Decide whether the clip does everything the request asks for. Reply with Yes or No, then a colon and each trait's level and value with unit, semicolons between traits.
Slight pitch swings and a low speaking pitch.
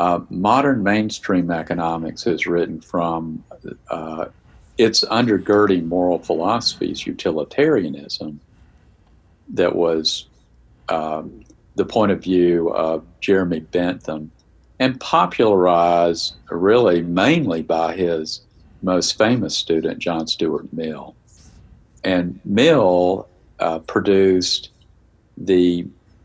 Yes: narrow, 2.3 semitones; very low, 85 Hz